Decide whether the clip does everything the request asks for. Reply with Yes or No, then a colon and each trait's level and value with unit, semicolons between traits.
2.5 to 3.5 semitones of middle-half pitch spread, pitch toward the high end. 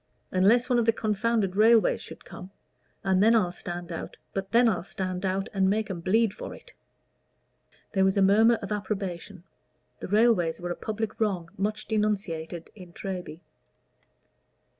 Yes: average, 3.1 semitones; high, 195 Hz